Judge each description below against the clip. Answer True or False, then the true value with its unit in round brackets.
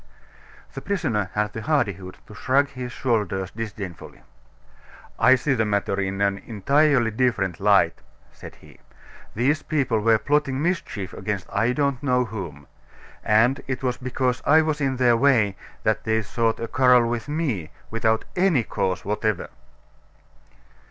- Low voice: True (115 Hz)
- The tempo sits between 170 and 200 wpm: False (145 wpm)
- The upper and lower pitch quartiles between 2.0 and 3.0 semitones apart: False (4.4 semitones)